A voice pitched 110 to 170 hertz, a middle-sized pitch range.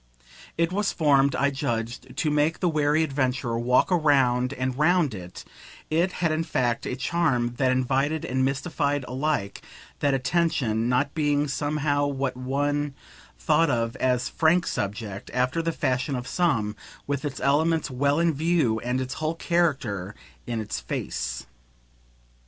Yes: medium, 140 Hz; average, 3.9 semitones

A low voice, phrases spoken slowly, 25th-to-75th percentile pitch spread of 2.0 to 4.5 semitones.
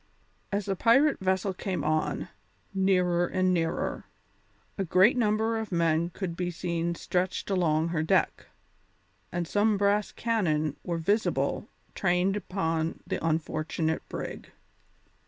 No: medium, 180 Hz; slow, 125 wpm; average, 3.4 semitones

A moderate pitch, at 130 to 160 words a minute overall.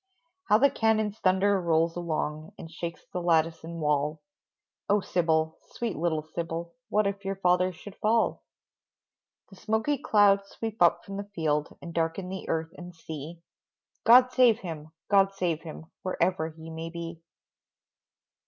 Yes: medium, 175 Hz; average, 155 wpm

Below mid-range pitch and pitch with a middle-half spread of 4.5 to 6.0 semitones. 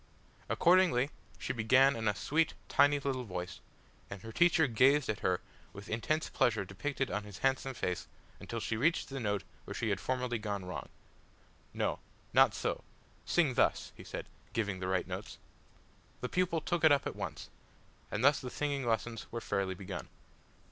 Yes: low, 120 Hz; wide, 5.6 semitones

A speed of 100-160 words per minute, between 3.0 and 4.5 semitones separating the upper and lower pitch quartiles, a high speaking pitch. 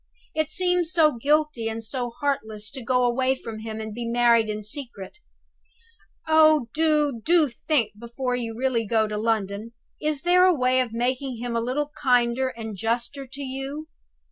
No: average, 170 wpm; average, 4.1 semitones; very high, 250 Hz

